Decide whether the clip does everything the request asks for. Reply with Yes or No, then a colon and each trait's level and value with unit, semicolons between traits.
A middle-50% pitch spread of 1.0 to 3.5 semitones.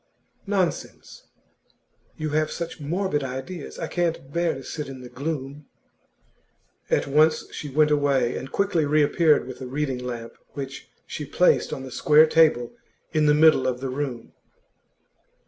Yes: average, 3.0 semitones